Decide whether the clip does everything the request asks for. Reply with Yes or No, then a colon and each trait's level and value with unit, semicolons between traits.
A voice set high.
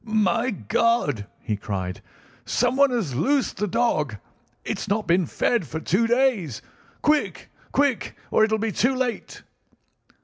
Yes: high, 220 Hz